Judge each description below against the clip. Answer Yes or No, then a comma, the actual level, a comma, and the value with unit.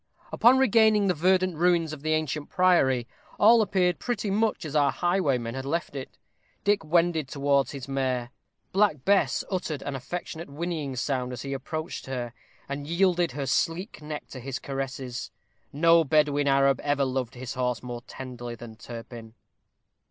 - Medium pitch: Yes, medium, 145 Hz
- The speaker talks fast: No, average, 160 wpm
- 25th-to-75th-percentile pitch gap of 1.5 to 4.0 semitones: No, average, 5.0 semitones